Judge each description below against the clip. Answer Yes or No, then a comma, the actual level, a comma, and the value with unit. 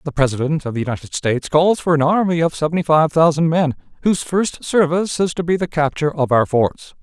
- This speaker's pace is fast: Yes, fast, 220 wpm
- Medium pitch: Yes, medium, 155 Hz